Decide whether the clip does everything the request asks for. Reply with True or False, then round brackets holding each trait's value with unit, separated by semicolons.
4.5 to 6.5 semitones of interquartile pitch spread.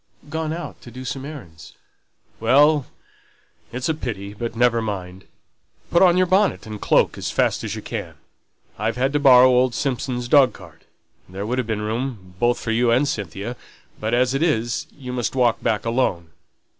False (3.7 semitones)